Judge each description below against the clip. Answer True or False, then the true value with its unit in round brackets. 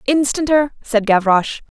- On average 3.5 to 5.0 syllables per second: True (4.7 syllables/s)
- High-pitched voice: True (250 Hz)